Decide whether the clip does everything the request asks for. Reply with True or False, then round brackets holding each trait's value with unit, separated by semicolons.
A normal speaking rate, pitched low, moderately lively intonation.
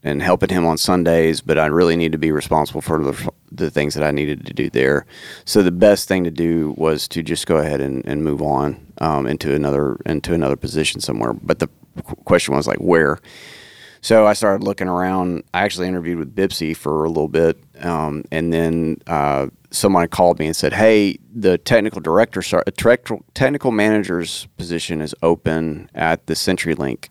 True (190 wpm; 80 Hz; 3.2 semitones)